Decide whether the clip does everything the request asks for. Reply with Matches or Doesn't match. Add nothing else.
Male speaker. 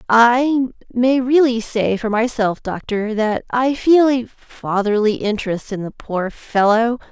Doesn't match